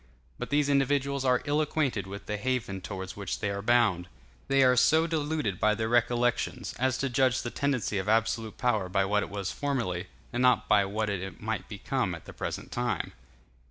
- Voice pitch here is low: Yes, low, 120 Hz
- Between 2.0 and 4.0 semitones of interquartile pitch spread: No, average, 4.7 semitones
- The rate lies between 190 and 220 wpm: Yes, average, 195 wpm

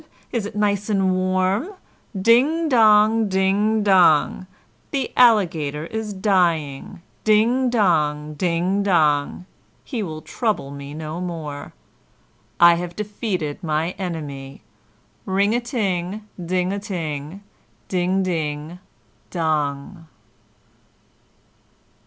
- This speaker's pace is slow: Yes, slow, 100 wpm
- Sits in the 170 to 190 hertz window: Yes, medium, 185 Hz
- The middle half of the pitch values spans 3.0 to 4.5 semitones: No, average, 5.0 semitones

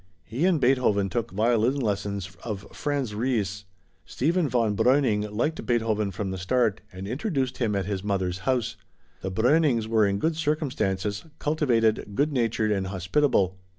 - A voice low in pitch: Yes, low, 110 Hz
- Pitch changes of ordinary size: Yes, average, 4.7 semitones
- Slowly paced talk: No, average, 150 wpm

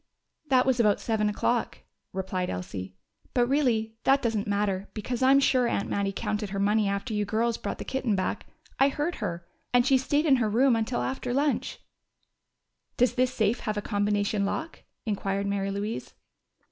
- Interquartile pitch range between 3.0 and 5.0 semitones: Yes, average, 4.0 semitones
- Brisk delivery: No, average, 175 wpm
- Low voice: No, high, 220 Hz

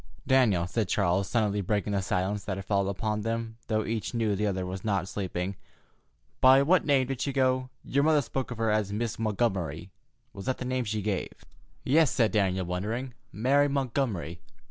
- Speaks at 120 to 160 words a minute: No, average, 190 wpm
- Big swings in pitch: No, average, 4.7 semitones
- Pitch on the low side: Yes, low, 110 Hz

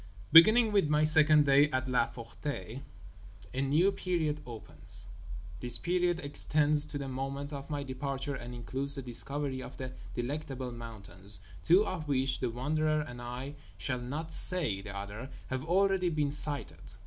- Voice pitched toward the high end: No, medium, 140 Hz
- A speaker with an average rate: Yes, average, 150 wpm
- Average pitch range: Yes, average, 3.8 semitones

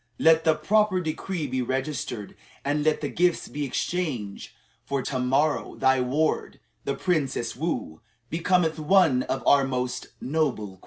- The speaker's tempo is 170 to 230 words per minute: No, average, 150 wpm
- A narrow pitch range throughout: No, average, 4.1 semitones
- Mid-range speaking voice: Yes, medium, 145 Hz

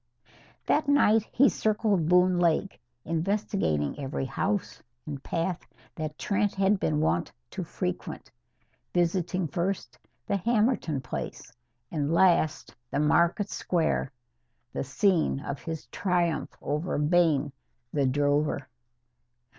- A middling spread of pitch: Yes, average, 4.9 semitones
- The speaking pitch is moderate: Yes, medium, 170 Hz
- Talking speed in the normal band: No, slow, 115 wpm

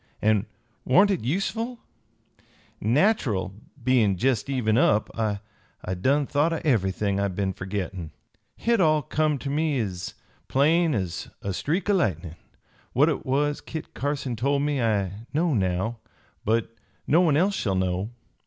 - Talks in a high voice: No, low, 125 Hz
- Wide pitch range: Yes, wide, 7.1 semitones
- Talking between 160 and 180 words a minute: No, average, 145 wpm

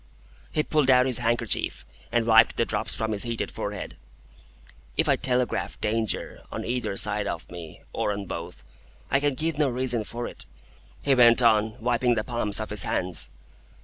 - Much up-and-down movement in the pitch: No, average, 3.1 semitones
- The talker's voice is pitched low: Yes, low, 115 Hz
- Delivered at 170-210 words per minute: Yes, average, 180 wpm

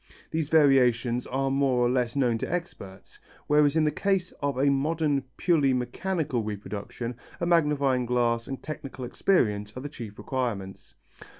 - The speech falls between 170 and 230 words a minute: No, average, 155 wpm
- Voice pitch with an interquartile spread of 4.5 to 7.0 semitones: No, average, 3.7 semitones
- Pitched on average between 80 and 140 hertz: Yes, low, 135 Hz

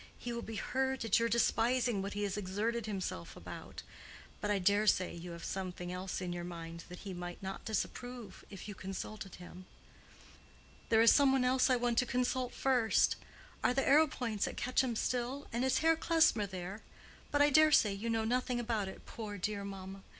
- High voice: Yes, high, 220 Hz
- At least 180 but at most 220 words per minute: Yes, average, 195 wpm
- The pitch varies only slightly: No, average, 4.6 semitones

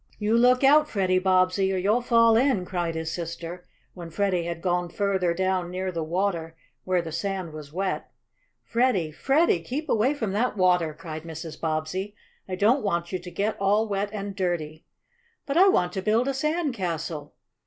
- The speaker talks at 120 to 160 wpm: No, average, 185 wpm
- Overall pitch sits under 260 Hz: Yes, medium, 185 Hz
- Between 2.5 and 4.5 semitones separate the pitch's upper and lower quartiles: Yes, average, 4.1 semitones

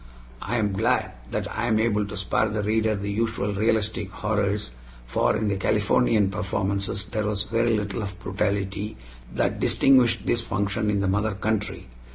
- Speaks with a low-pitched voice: Yes, low, 105 Hz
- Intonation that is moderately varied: No, narrow, 1.8 semitones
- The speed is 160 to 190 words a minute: Yes, average, 175 wpm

